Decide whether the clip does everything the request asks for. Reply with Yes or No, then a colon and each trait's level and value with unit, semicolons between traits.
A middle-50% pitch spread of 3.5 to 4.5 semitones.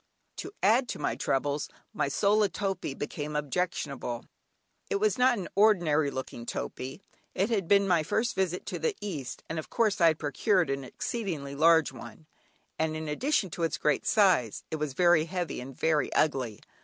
No: wide, 5.4 semitones